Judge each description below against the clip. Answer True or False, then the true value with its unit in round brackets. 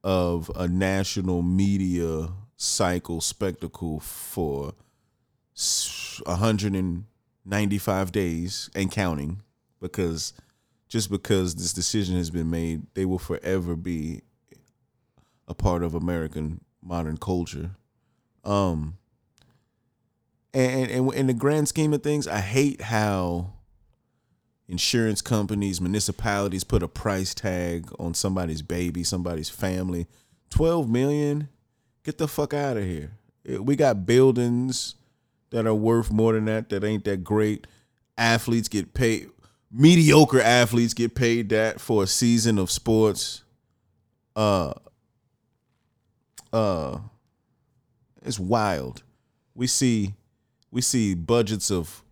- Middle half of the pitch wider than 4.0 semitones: True (4.9 semitones)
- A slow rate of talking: True (110 wpm)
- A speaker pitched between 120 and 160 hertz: False (105 Hz)